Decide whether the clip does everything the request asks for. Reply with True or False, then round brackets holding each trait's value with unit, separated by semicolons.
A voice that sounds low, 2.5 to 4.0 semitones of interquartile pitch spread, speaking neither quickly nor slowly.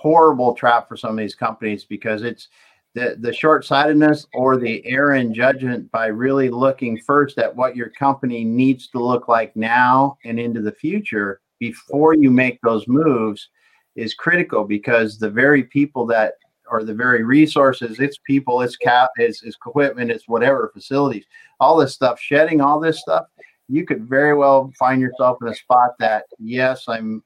True (125 Hz; 3.3 semitones; 170 wpm)